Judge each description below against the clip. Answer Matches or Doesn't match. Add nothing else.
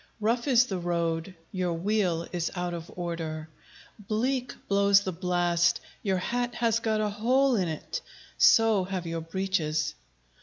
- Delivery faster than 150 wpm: Doesn't match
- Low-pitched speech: Doesn't match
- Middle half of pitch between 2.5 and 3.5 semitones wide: Doesn't match